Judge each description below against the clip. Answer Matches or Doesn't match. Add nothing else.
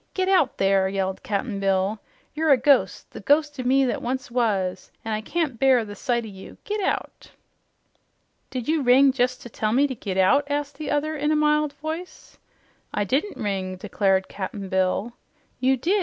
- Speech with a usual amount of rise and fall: Doesn't match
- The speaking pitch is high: Matches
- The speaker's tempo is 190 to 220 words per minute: Matches